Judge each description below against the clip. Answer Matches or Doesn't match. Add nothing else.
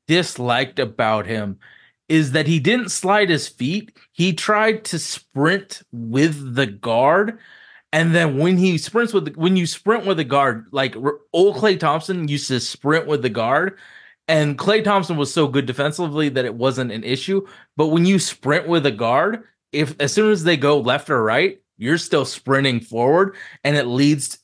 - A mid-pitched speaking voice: Matches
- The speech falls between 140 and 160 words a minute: Doesn't match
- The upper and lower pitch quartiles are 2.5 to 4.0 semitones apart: Doesn't match